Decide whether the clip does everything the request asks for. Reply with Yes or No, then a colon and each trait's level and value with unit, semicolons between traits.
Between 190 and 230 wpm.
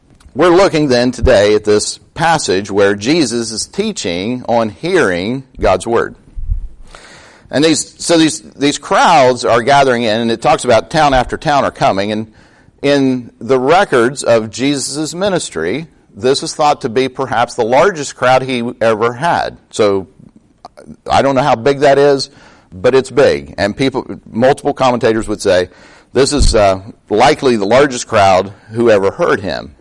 No: average, 160 wpm